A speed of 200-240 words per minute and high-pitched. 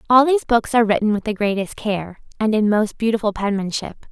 Yes: fast, 205 wpm; high, 215 Hz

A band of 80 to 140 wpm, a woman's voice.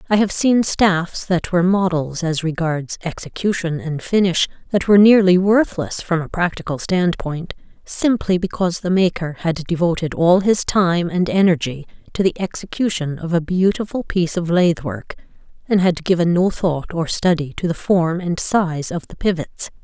No: average, 170 wpm; female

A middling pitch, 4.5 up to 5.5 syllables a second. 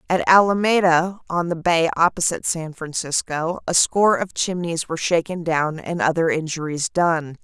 Yes: medium, 170 Hz; 4.9 syllables/s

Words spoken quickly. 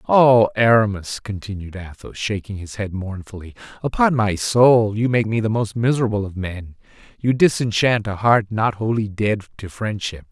No: average, 165 wpm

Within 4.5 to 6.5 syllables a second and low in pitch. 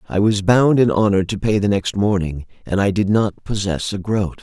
Yes: 5.1 syllables/s; low, 100 Hz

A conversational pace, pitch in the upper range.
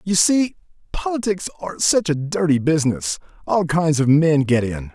No: average, 160 wpm; medium, 160 Hz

